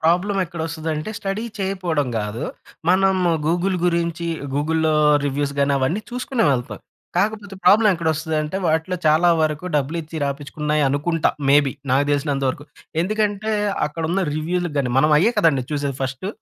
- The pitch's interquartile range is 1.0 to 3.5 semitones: No, average, 4.0 semitones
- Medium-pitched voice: Yes, medium, 160 Hz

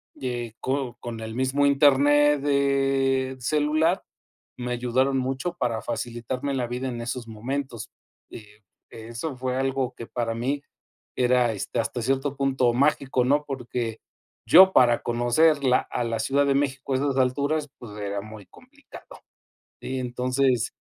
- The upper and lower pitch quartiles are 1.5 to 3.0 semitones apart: Yes, narrow, 2.6 semitones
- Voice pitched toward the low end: Yes, low, 130 Hz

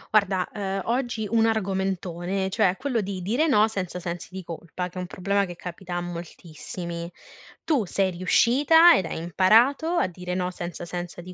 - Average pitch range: Yes, average, 3.7 semitones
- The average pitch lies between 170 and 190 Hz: Yes, medium, 185 Hz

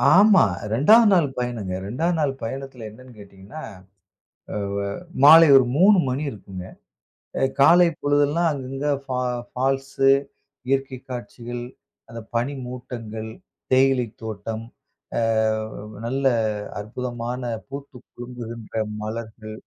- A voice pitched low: Yes, low, 125 Hz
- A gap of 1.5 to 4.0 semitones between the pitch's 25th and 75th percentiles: Yes, average, 3.6 semitones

